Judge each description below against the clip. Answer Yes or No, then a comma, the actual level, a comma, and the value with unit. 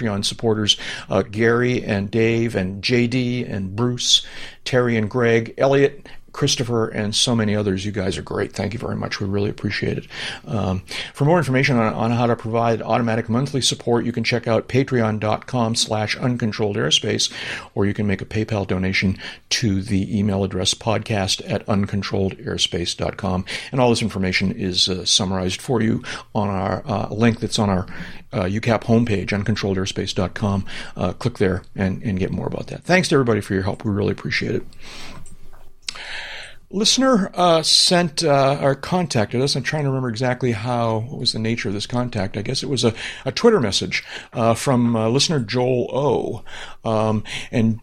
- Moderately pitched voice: No, low, 115 Hz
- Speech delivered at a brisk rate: No, average, 180 wpm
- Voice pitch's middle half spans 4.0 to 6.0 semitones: No, average, 3.5 semitones